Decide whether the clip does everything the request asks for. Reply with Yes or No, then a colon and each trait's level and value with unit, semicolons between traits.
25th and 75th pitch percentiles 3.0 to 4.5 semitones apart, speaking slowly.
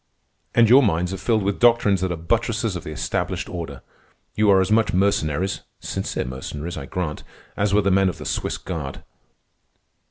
No: average, 4.1 semitones; average, 185 wpm